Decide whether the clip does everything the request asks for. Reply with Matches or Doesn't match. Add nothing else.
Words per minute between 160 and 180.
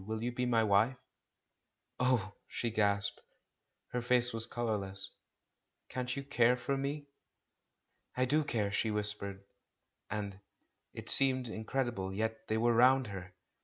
Doesn't match